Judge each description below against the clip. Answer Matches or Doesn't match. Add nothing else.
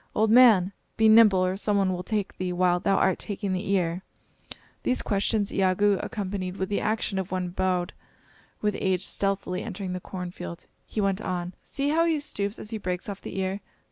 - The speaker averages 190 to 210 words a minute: Matches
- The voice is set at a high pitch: Matches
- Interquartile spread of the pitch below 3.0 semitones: Matches